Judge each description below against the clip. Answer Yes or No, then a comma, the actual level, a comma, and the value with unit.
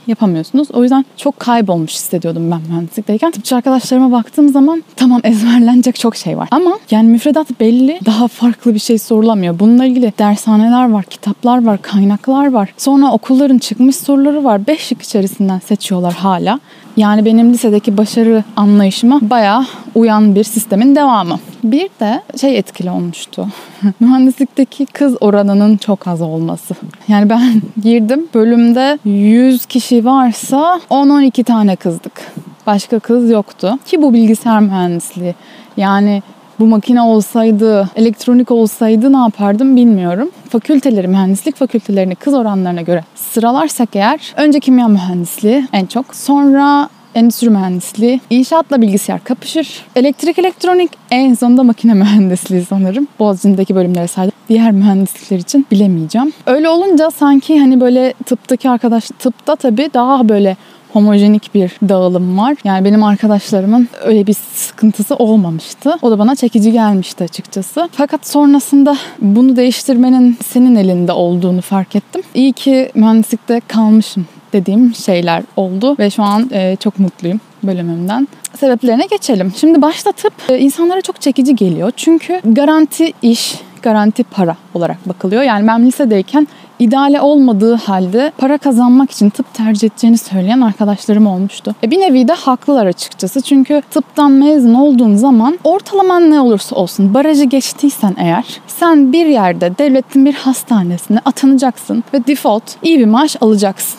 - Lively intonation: No, average, 4.7 semitones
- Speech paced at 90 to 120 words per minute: No, average, 135 wpm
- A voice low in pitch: No, high, 230 Hz